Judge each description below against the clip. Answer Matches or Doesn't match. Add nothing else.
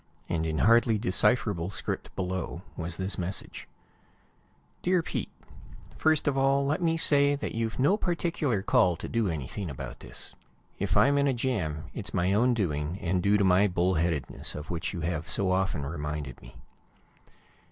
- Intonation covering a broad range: Matches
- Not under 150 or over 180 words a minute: Matches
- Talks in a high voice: Doesn't match